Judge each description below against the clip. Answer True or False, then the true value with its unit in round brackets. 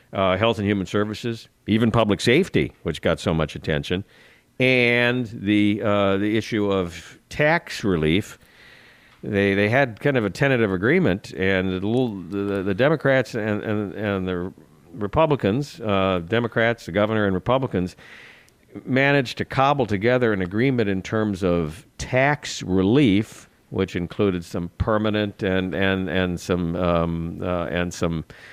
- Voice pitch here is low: True (105 Hz)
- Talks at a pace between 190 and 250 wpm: False (145 wpm)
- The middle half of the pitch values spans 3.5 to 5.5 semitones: True (3.9 semitones)